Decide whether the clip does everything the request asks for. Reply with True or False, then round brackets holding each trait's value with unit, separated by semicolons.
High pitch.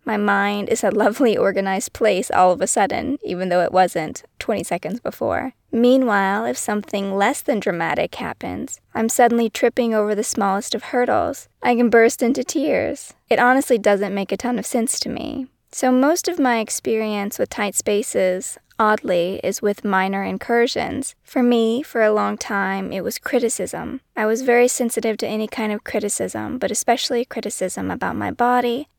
True (225 Hz)